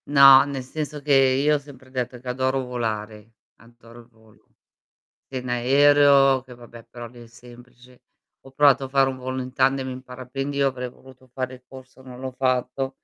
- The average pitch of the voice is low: Yes, low, 130 Hz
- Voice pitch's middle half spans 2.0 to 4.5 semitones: No, narrow, 1.6 semitones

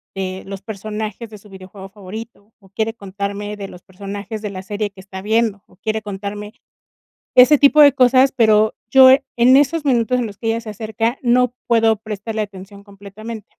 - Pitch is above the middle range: Yes, high, 215 Hz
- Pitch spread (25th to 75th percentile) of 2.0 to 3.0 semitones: Yes, average, 2.7 semitones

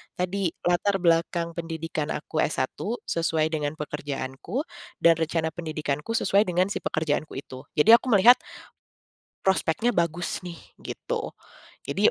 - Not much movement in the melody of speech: No, average, 3.2 semitones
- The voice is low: No, medium, 165 Hz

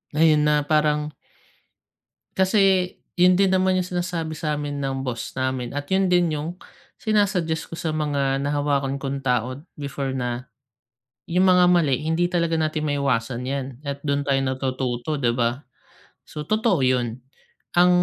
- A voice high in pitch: No, medium, 150 Hz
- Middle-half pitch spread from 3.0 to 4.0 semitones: No, average, 4.6 semitones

